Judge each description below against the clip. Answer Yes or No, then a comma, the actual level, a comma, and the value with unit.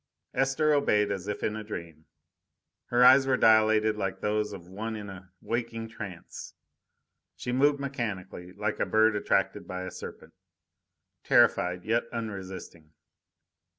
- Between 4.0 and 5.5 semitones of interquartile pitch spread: No, average, 3.6 semitones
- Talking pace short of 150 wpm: Yes, average, 140 wpm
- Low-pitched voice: Yes, low, 105 Hz